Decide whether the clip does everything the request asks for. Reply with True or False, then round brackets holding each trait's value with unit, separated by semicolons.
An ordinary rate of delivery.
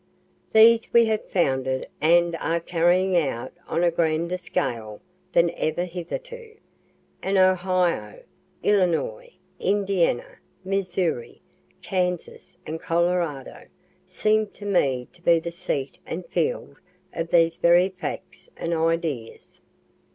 False (115 wpm)